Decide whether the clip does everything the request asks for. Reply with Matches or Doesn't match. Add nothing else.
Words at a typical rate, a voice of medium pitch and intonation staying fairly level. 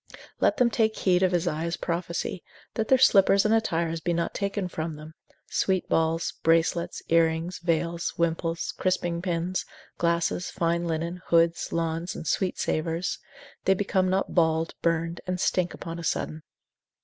Matches